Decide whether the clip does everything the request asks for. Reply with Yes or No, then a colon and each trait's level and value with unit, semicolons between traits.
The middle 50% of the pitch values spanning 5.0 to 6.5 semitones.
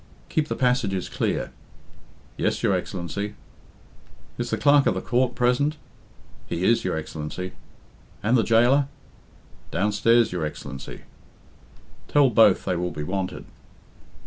Yes: wide, 5.4 semitones